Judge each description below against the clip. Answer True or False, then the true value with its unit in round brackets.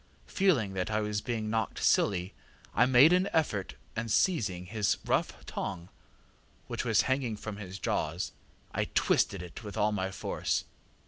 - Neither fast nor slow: True (155 wpm)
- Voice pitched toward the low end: True (105 Hz)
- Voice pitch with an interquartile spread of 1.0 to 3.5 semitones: False (4.1 semitones)